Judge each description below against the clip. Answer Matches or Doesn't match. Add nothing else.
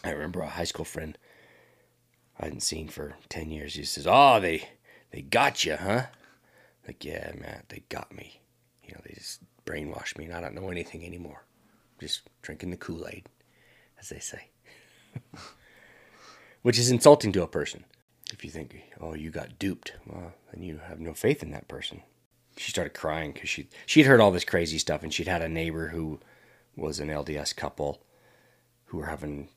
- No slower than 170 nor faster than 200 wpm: Matches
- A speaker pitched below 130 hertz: Matches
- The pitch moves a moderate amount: Matches